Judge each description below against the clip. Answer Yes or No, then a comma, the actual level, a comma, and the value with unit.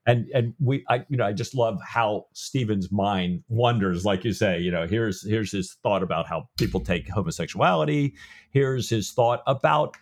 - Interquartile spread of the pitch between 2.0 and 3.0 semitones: No, average, 4.3 semitones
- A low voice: Yes, low, 115 Hz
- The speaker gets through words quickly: No, average, 185 wpm